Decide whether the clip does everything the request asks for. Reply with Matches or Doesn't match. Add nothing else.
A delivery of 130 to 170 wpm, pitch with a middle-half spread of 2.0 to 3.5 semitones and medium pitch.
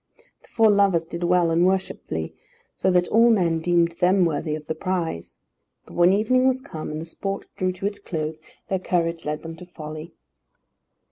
Doesn't match